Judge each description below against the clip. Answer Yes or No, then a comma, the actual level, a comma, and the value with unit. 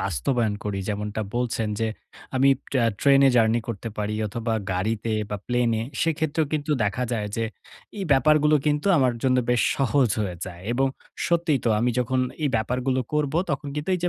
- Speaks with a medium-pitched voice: No, low, 125 Hz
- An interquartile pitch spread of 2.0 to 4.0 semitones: No, average, 4.4 semitones